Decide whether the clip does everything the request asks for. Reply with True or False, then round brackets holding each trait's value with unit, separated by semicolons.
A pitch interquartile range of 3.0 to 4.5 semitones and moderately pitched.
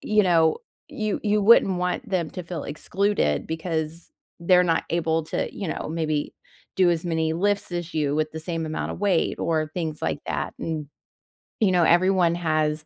False (2.6 semitones; 170 Hz)